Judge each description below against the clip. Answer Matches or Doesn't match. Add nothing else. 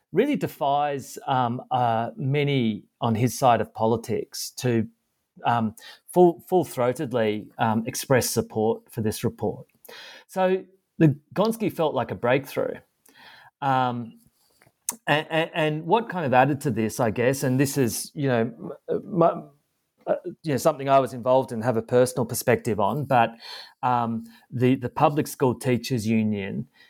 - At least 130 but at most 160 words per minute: Matches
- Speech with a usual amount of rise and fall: Matches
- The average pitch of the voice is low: Matches